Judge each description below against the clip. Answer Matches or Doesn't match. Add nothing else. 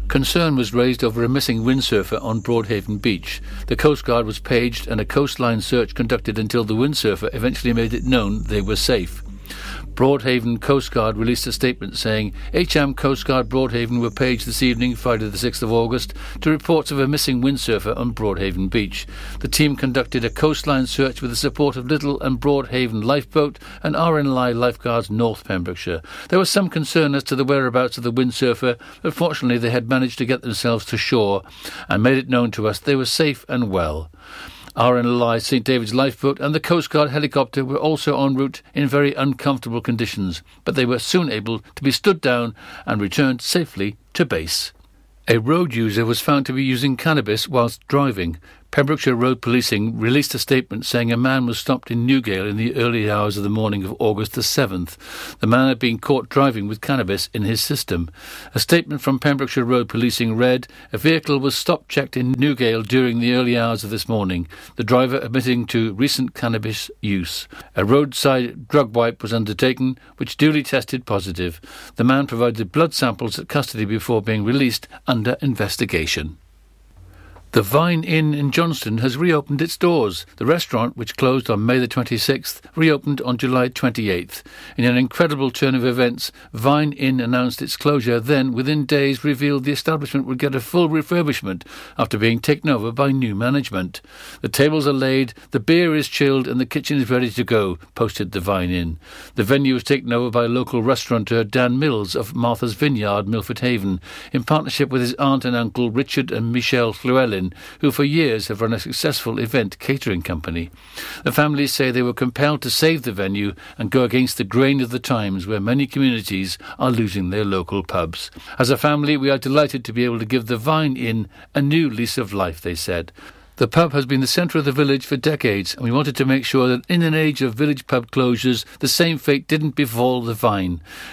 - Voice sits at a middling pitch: Doesn't match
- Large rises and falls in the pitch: Doesn't match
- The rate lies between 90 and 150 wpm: Doesn't match